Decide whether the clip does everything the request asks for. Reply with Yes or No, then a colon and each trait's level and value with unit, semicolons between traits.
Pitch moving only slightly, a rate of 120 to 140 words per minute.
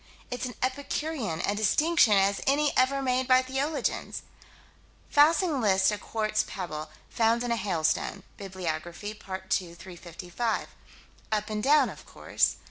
No: wide, 5.6 semitones; slow, 135 wpm